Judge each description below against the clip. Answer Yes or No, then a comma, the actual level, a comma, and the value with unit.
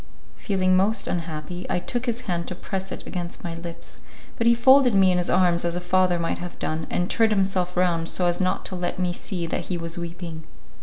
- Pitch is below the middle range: No, medium, 180 Hz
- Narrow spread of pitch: Yes, narrow, 1.9 semitones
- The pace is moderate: No, fast, 225 wpm